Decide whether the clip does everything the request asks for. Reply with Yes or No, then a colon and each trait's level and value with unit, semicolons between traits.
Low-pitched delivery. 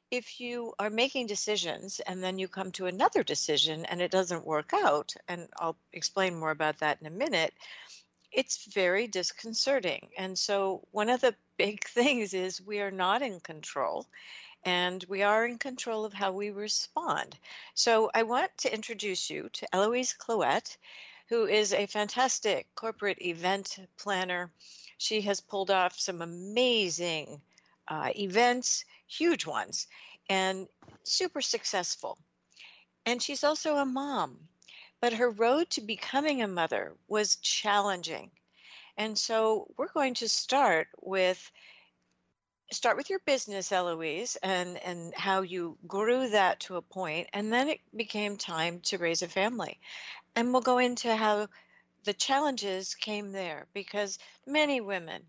No: high, 205 Hz